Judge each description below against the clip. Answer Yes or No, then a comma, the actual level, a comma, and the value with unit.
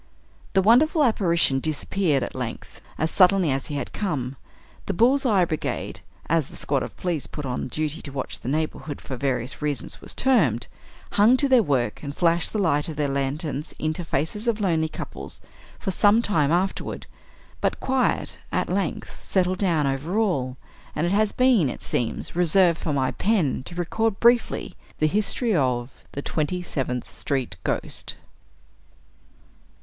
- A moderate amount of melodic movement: No, wide, 6.2 semitones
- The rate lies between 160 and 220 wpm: Yes, average, 165 wpm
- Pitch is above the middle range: No, medium, 160 Hz